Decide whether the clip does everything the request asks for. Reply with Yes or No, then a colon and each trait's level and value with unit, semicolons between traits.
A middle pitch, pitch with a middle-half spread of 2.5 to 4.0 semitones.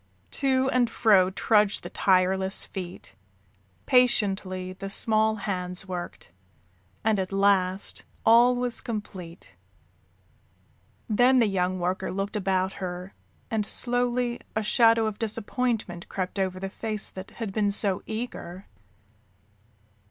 No: high, 200 Hz; average, 3.4 semitones